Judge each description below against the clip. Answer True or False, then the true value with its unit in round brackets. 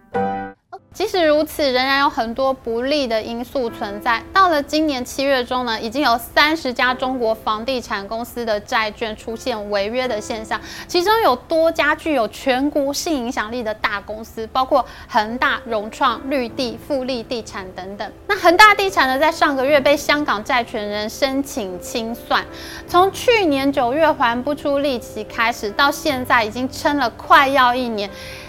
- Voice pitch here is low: False (260 Hz)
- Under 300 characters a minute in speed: True (255 characters per minute)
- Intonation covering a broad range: False (4.5 semitones)